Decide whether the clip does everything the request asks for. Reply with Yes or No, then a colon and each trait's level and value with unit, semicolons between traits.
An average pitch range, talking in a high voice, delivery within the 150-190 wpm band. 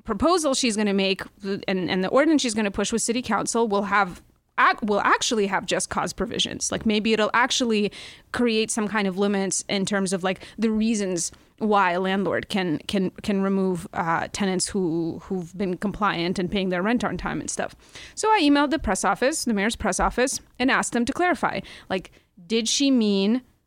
No: average, 3.2 semitones; high, 205 Hz; average, 200 wpm